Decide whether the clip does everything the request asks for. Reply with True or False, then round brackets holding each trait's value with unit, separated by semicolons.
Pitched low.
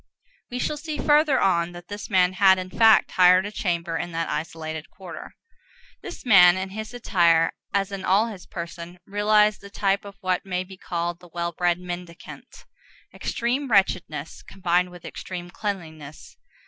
False (185 Hz)